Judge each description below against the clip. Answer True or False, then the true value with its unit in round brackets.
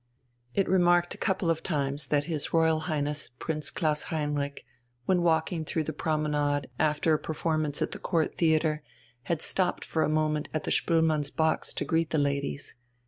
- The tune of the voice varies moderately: False (1.8 semitones)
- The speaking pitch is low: False (155 Hz)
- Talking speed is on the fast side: False (175 wpm)